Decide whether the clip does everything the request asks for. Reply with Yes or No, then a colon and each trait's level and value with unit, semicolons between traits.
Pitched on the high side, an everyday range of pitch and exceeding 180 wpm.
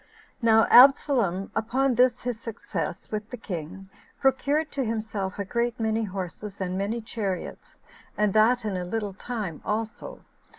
No: high, 220 Hz; average, 3.7 semitones; average, 155 wpm